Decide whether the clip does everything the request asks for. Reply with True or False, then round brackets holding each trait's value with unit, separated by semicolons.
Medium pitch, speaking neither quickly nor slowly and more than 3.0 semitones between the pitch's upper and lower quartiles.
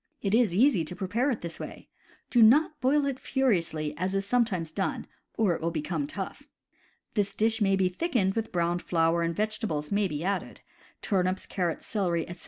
False (195 Hz; 190 wpm; 5.0 semitones)